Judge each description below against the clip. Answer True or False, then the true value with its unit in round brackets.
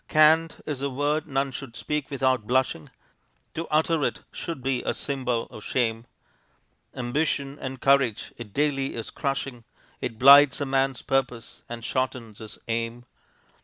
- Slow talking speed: False (150 wpm)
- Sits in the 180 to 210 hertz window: False (135 Hz)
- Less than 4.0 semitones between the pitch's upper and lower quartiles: True (3.0 semitones)